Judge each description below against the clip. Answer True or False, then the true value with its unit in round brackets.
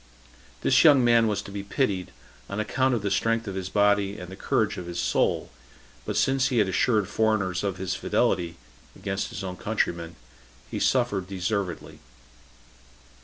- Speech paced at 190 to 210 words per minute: False (170 wpm)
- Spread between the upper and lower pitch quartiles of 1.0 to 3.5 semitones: True (3.2 semitones)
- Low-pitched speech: True (100 Hz)